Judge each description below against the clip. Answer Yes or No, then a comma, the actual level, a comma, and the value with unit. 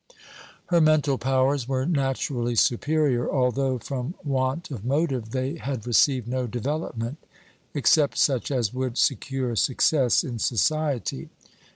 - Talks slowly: Yes, slow, 125 wpm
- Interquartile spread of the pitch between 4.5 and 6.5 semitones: No, average, 2.7 semitones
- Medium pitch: No, low, 130 Hz